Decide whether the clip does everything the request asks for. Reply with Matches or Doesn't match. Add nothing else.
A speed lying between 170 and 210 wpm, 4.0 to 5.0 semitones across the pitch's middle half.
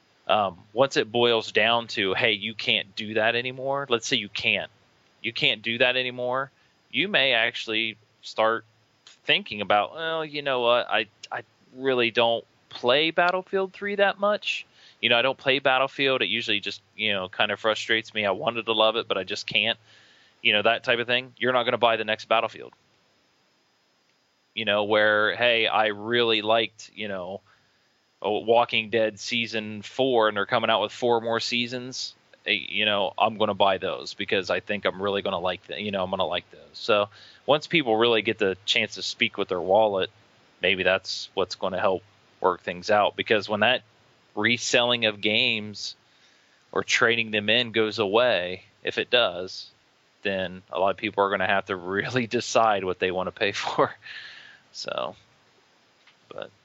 Doesn't match